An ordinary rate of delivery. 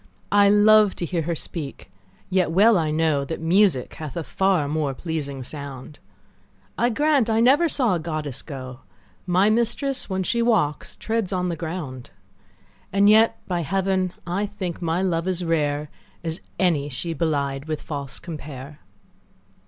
Yes: average, 160 wpm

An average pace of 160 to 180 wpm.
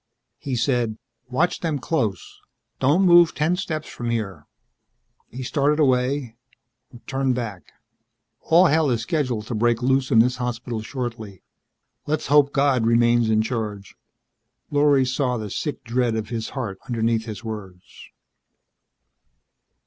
No: slow, 135 wpm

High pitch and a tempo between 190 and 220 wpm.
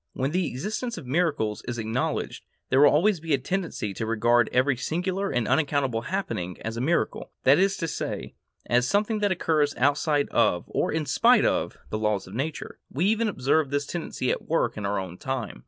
No: medium, 140 Hz; average, 200 wpm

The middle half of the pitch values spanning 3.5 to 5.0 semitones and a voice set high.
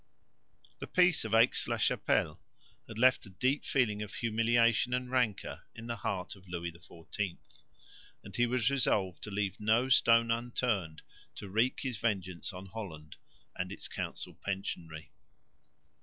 No: average, 4.1 semitones; low, 110 Hz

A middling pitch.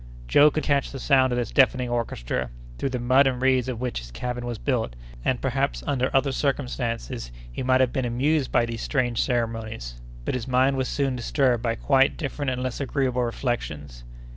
No: low, 125 Hz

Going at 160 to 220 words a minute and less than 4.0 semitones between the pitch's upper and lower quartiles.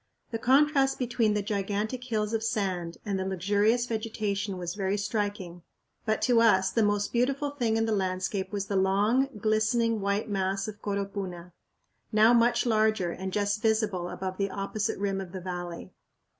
Yes: average, 170 wpm; average, 2.7 semitones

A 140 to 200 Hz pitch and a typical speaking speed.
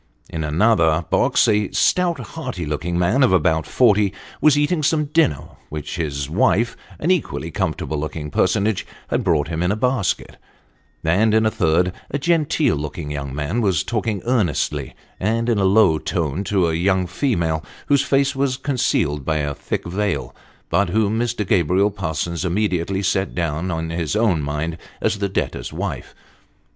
No: very low, 95 Hz; average, 165 wpm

